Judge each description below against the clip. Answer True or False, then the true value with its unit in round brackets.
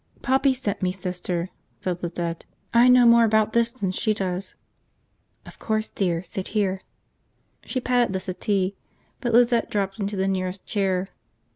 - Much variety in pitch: False (4.0 semitones)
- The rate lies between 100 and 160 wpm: True (155 wpm)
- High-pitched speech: True (200 Hz)